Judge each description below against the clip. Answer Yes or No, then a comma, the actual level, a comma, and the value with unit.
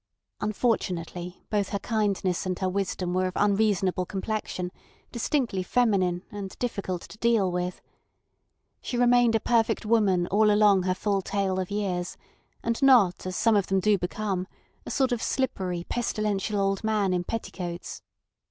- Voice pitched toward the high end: Yes, high, 200 Hz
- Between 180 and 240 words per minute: No, average, 150 wpm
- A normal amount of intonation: Yes, average, 3.0 semitones